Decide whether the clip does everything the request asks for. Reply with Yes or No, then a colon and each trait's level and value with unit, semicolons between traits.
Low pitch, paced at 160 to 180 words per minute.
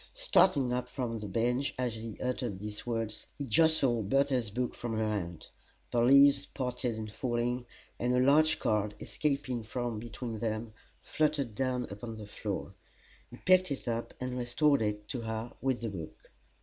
Yes: low, 120 Hz; average, 170 wpm